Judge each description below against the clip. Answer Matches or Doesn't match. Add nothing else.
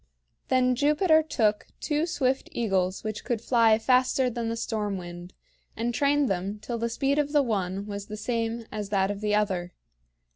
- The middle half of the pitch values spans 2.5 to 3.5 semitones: Doesn't match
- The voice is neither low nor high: Doesn't match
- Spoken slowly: Doesn't match